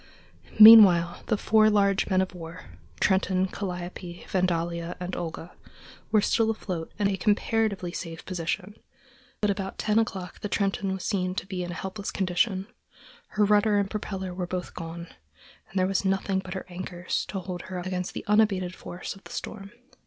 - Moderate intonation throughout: No, narrow, 2.3 semitones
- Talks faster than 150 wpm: Yes, average, 180 wpm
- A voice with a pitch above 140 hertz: Yes, high, 190 Hz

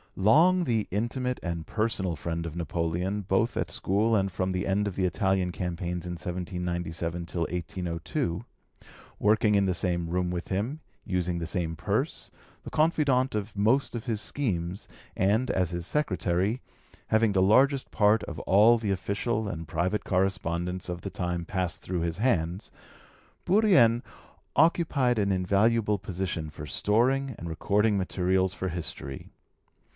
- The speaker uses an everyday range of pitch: Yes, average, 4.1 semitones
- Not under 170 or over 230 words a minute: No, average, 150 wpm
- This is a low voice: Yes, very low, 95 Hz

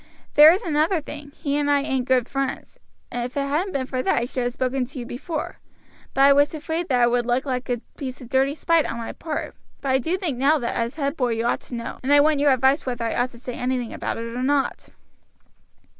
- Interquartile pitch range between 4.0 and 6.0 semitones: No, average, 3.0 semitones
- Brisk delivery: Yes, fast, 255 wpm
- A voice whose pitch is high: Yes, very high, 265 Hz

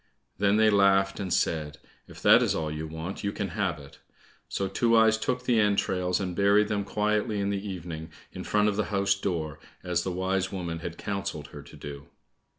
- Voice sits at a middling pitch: No, very low, 95 Hz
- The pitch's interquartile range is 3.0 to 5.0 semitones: Yes, average, 3.3 semitones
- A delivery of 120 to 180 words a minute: No, average, 200 wpm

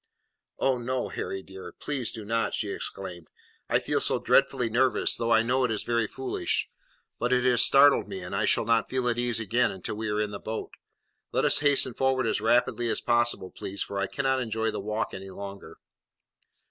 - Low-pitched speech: Yes, low, 115 Hz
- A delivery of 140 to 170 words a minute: No, fast, 205 wpm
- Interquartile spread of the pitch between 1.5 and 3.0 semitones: No, average, 3.6 semitones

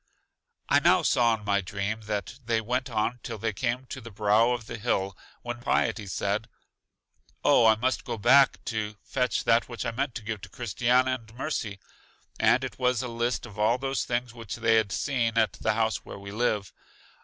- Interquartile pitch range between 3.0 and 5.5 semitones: No, narrow, 2.4 semitones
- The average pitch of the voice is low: Yes, low, 115 Hz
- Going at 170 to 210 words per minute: Yes, average, 200 wpm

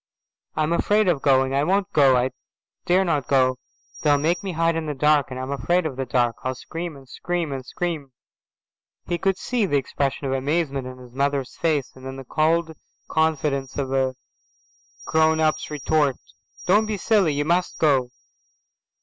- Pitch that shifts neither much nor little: Yes, average, 3.9 semitones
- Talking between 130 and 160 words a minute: No, average, 175 wpm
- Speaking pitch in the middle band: Yes, medium, 145 Hz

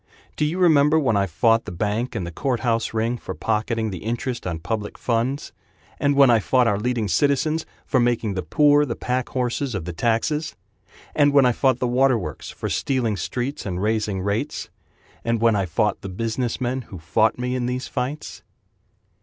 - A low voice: Yes, low, 120 Hz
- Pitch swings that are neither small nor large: Yes, average, 3.7 semitones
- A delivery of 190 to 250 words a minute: Yes, average, 195 wpm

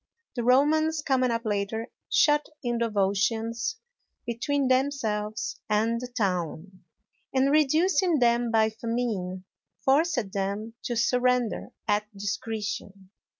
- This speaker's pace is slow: Yes, slow, 110 wpm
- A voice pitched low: No, high, 230 Hz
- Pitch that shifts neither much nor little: Yes, average, 3.8 semitones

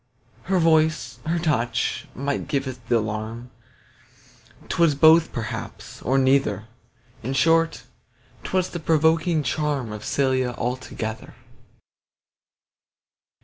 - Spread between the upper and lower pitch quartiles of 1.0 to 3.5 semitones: No, average, 4.9 semitones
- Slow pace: Yes, slow, 100 wpm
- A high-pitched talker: No, low, 135 Hz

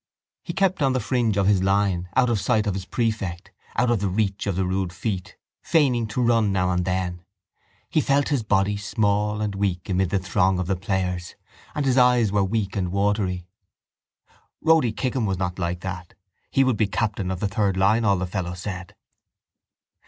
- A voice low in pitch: Yes, low, 100 Hz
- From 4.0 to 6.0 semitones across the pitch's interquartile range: No, average, 3.5 semitones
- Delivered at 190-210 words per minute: Yes, average, 195 wpm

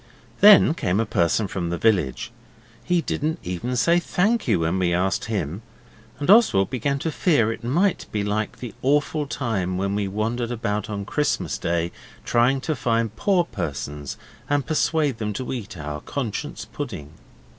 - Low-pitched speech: Yes, low, 115 Hz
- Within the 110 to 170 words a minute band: Yes, average, 165 wpm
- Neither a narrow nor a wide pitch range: No, wide, 7.2 semitones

